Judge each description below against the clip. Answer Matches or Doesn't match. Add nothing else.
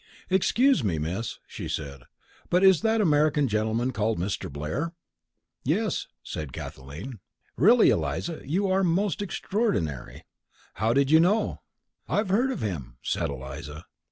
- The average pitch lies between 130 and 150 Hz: Matches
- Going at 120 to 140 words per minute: Matches